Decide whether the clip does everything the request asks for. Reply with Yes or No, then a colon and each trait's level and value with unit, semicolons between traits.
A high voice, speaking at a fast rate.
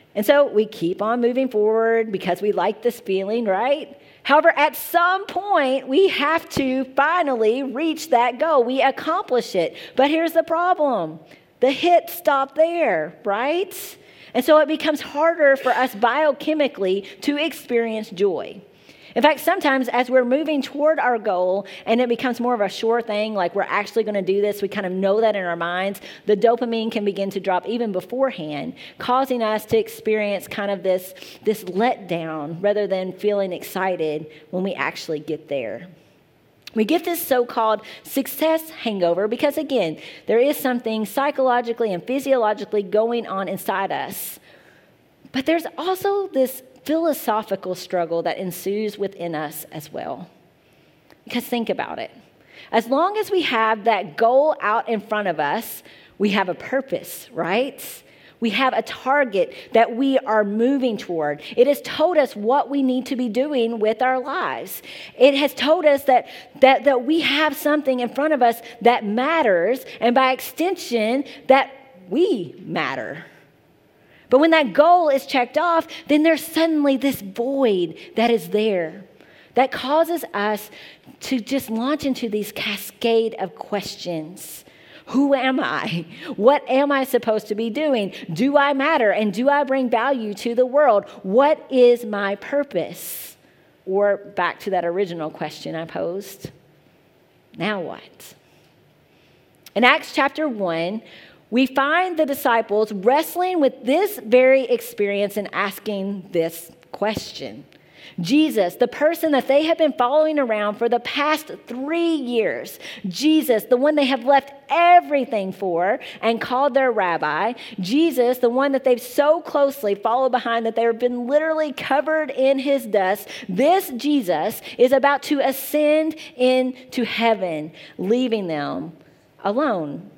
No: high, 245 Hz; average, 155 wpm